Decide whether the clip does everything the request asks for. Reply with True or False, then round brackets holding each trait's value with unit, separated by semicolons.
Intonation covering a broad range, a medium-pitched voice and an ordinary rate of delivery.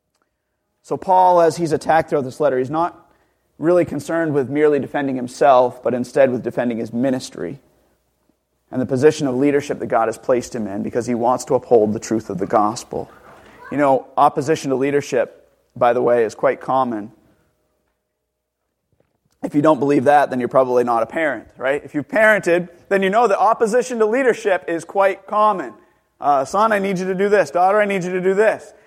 True (6.6 semitones; 145 Hz; 195 wpm)